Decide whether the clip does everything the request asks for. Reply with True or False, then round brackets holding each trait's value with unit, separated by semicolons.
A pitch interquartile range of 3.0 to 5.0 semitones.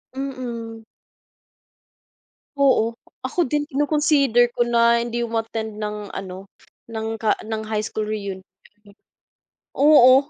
True (3.5 semitones)